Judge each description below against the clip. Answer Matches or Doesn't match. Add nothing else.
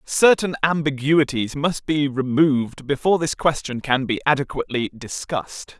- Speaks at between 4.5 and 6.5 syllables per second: Matches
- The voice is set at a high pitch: Doesn't match